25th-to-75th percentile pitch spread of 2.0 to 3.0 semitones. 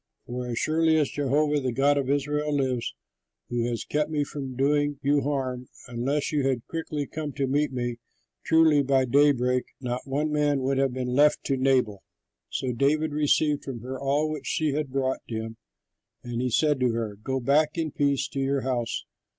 Yes: average, 2.7 semitones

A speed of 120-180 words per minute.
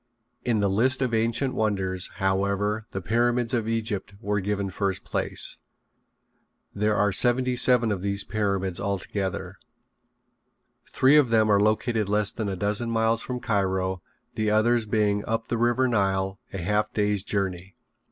Yes: average, 150 wpm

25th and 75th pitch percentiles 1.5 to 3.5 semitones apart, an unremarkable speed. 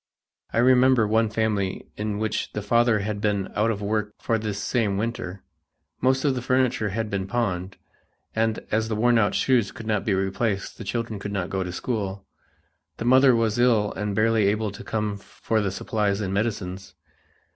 Yes: narrow, 2.4 semitones; average, 190 wpm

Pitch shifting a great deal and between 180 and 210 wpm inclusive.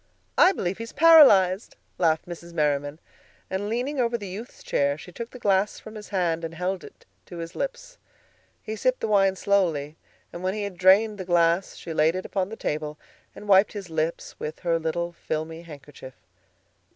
No: average, 4.2 semitones; average, 190 wpm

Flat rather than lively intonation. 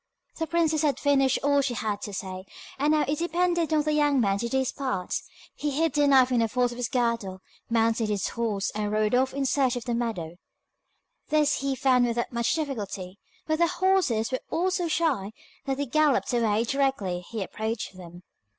No: average, 5.1 semitones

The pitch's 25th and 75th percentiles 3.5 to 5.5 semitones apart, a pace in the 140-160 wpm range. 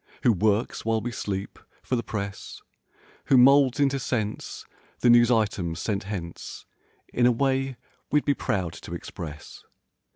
Yes: average, 4.3 semitones; average, 150 wpm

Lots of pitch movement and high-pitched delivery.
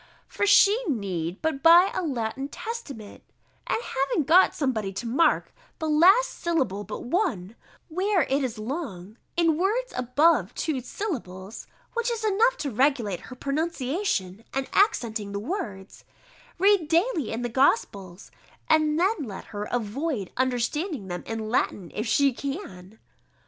Yes: wide, 7.9 semitones; very high, 270 Hz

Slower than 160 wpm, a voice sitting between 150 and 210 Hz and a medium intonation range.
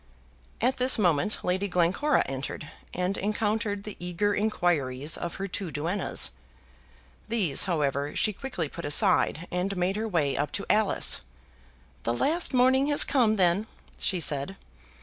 Yes: average, 145 wpm; high, 190 Hz; average, 4.7 semitones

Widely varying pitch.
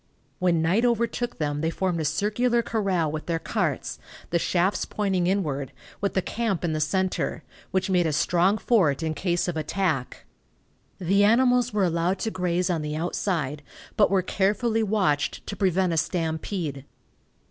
No: average, 4.0 semitones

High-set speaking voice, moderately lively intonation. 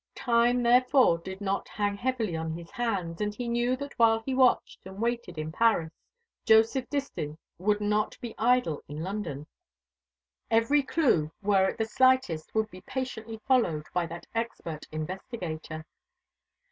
No: high, 215 Hz; wide, 6.1 semitones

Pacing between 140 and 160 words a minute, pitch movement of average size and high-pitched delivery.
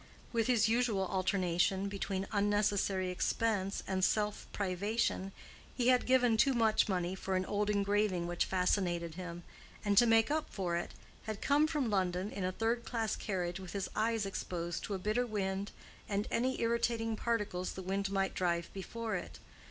No: average, 170 wpm; average, 3.3 semitones; high, 200 Hz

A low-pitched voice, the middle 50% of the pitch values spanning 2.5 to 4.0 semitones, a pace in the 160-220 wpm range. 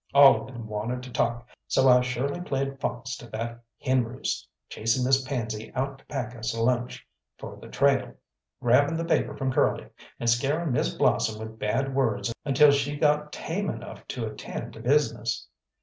Yes: low, 125 Hz; average, 2.9 semitones; average, 180 wpm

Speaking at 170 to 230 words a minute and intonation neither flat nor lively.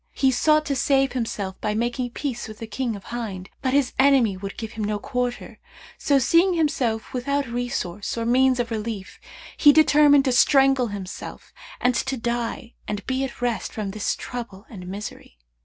Yes: average, 180 wpm; average, 3.9 semitones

